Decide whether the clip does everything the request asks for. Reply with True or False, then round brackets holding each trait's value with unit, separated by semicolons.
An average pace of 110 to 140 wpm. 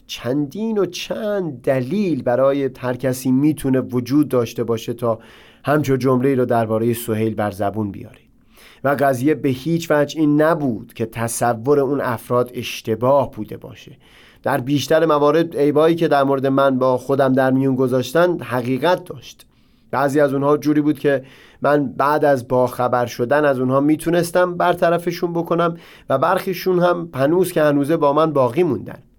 False (155 wpm)